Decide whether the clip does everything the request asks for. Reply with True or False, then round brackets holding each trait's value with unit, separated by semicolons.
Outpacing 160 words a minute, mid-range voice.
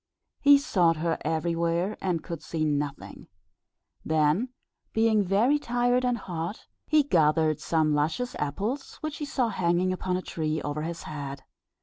False (145 wpm; 170 Hz)